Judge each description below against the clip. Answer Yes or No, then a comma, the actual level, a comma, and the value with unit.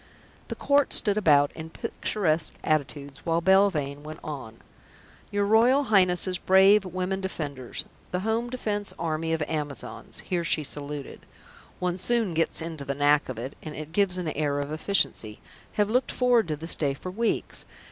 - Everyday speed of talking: Yes, average, 165 wpm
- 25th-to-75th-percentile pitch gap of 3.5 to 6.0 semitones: Yes, average, 5.3 semitones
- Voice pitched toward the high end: No, medium, 165 Hz